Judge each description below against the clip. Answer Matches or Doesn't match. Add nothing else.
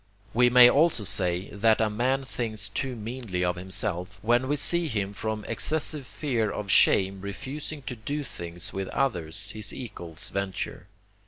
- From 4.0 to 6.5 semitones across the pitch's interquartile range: Matches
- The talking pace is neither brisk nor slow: Matches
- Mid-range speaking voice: Doesn't match